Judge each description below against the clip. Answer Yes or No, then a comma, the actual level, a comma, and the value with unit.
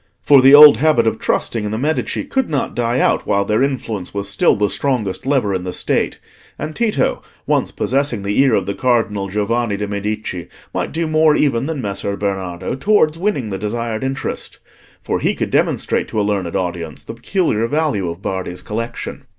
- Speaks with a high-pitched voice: No, low, 115 Hz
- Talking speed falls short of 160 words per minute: No, average, 190 wpm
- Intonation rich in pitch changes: Yes, wide, 5.7 semitones